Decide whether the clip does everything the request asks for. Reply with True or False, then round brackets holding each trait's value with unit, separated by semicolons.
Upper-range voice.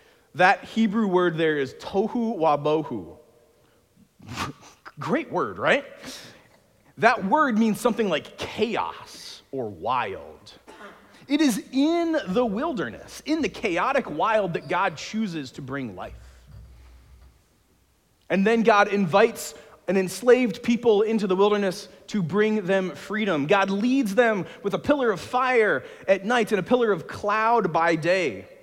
True (210 Hz)